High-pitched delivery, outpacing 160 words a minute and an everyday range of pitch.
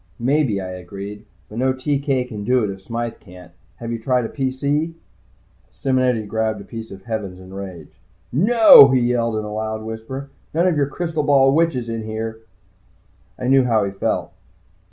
No: low, 115 Hz; average, 185 wpm; average, 4.1 semitones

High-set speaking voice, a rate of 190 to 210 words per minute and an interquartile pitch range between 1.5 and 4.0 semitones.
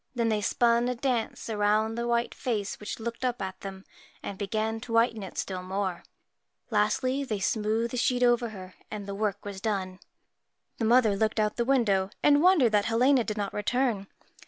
Yes: high, 220 Hz; average, 195 wpm; average, 2.9 semitones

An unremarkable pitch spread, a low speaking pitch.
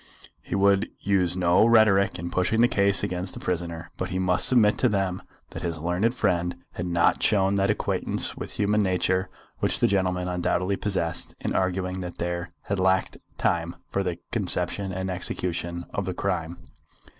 No: narrow, 2.0 semitones; very low, 95 Hz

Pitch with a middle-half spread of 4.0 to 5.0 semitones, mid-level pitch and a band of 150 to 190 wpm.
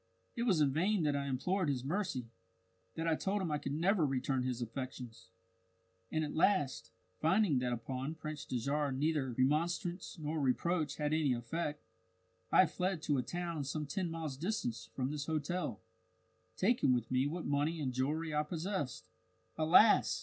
Yes: average, 4.3 semitones; medium, 150 Hz; average, 165 wpm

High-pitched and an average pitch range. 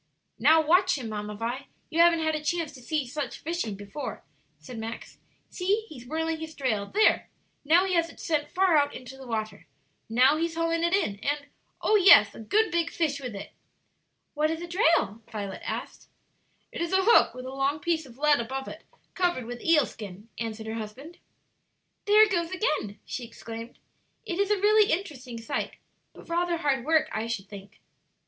No: very high, 295 Hz; wide, 6.7 semitones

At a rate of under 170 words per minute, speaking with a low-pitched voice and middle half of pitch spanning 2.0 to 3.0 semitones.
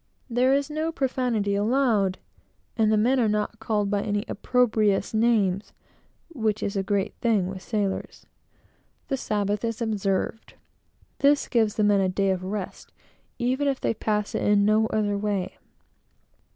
No: average, 155 wpm; high, 215 Hz; average, 2.7 semitones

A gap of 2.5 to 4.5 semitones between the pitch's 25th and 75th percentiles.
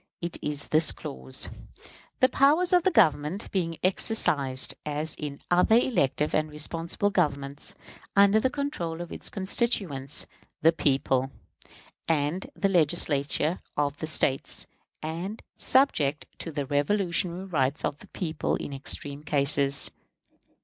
No: average, 5.0 semitones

